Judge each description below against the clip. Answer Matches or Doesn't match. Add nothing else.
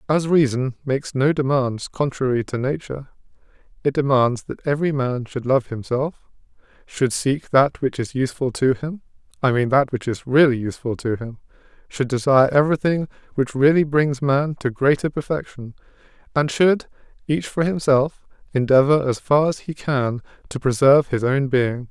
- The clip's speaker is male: Matches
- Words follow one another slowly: Doesn't match